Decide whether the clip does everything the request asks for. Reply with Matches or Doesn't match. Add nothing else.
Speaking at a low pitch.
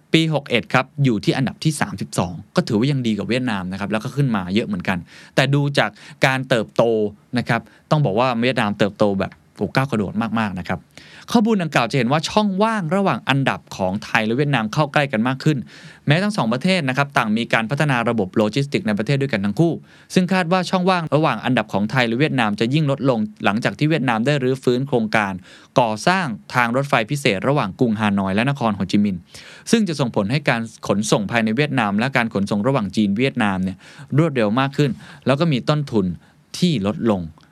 Matches